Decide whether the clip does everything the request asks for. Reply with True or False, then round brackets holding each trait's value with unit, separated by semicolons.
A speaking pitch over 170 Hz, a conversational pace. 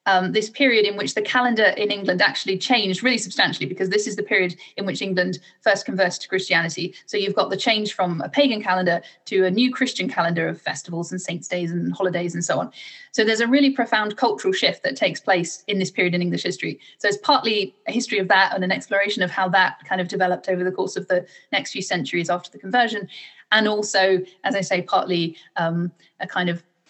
False (190 Hz; 230 wpm)